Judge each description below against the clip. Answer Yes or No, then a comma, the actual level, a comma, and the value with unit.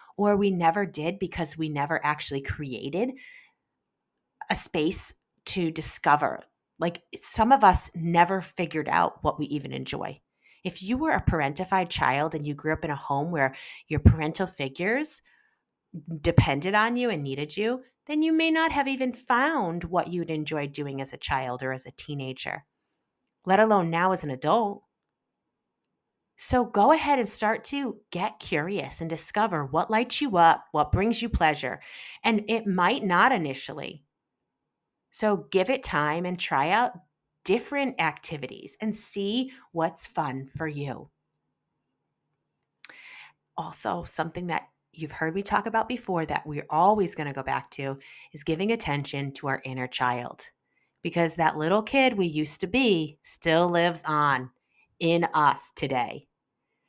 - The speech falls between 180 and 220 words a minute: No, average, 155 wpm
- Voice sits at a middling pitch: Yes, medium, 170 Hz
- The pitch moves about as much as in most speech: No, wide, 6.1 semitones